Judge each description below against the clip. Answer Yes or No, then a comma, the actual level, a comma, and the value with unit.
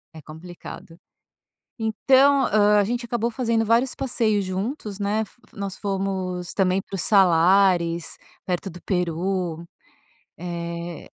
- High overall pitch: Yes, high, 195 Hz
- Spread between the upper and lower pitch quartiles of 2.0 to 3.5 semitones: No, average, 3.9 semitones